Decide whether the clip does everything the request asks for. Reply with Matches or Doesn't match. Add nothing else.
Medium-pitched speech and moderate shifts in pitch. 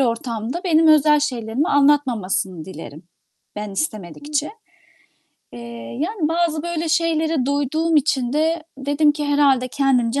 Doesn't match